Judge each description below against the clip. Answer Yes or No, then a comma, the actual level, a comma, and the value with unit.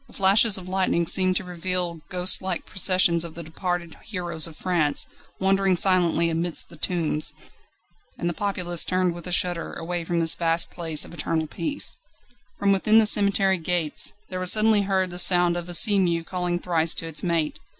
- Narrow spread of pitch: Yes, narrow, 1.9 semitones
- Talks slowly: No, average, 185 wpm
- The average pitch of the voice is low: No, medium, 175 Hz